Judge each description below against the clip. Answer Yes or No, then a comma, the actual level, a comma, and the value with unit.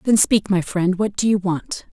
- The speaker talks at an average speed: No, fast, 240 wpm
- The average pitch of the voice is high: Yes, high, 195 Hz